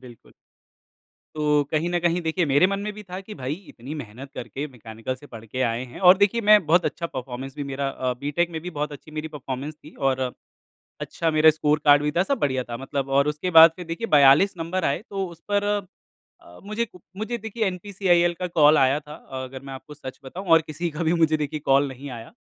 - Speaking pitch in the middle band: Yes, medium, 150 Hz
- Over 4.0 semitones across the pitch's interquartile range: Yes, average, 4.5 semitones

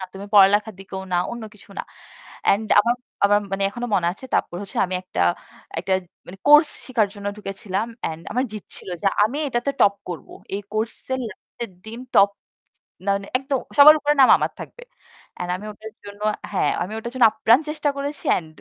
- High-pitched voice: Yes, high, 210 Hz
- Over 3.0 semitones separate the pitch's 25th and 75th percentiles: Yes, average, 3.7 semitones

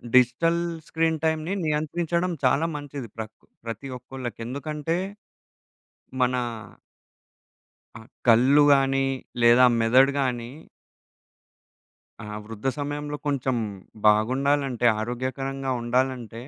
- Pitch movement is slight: No, average, 3.3 semitones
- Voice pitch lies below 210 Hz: Yes, low, 135 Hz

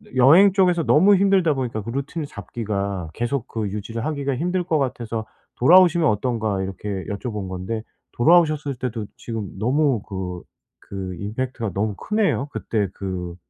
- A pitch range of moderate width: No, wide, 7.0 semitones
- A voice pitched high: No, low, 120 Hz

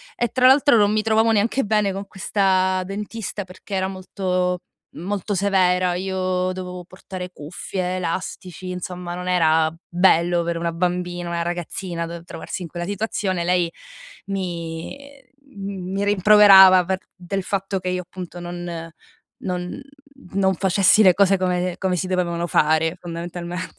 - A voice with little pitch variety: Yes, narrow, 1.9 semitones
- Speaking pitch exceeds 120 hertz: Yes, medium, 185 Hz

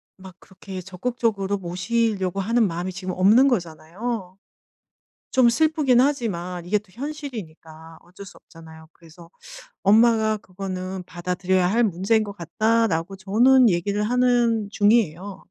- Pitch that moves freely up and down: No, average, 4.3 semitones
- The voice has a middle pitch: No, high, 195 Hz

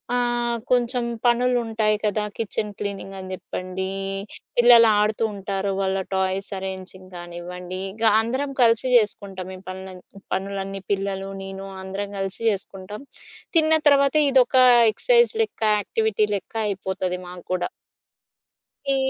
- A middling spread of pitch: Yes, average, 3.6 semitones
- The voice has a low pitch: No, high, 200 Hz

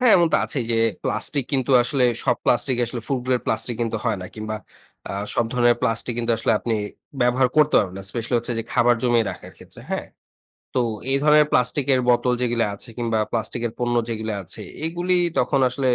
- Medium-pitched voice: No, low, 120 Hz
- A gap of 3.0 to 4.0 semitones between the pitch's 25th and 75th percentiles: No, narrow, 2.5 semitones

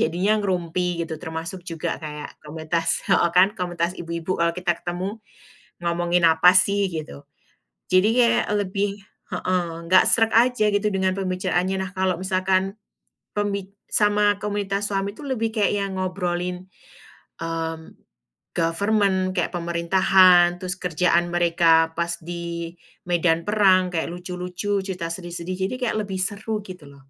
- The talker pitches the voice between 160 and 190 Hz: Yes, medium, 185 Hz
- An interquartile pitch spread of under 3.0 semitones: Yes, narrow, 2.6 semitones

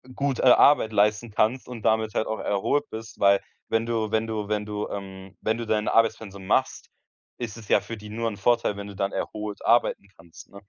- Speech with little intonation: Yes, narrow, 2.1 semitones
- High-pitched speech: No, low, 110 Hz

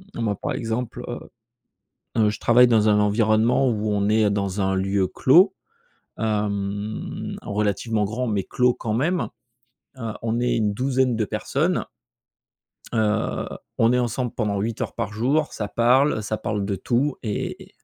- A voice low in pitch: Yes, low, 110 Hz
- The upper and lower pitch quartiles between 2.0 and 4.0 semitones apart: Yes, average, 2.8 semitones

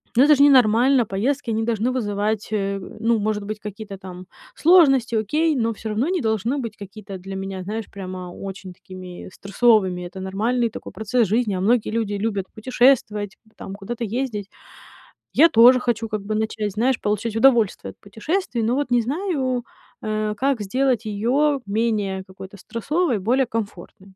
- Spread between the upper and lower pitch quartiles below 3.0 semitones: No, average, 3.7 semitones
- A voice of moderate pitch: No, high, 220 Hz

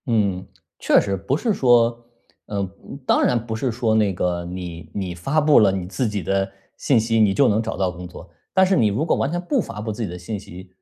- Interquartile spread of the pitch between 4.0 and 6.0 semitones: Yes, average, 4.5 semitones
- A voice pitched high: No, low, 105 Hz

